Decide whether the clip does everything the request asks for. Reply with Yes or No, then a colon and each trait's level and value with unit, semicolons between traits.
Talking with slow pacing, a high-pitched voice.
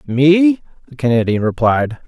No: slow, 115 wpm; low, 135 Hz